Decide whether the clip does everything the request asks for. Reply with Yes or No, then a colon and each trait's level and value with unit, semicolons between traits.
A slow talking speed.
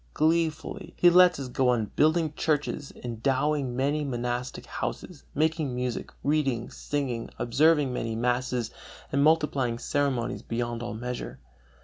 Yes: slow, 125 wpm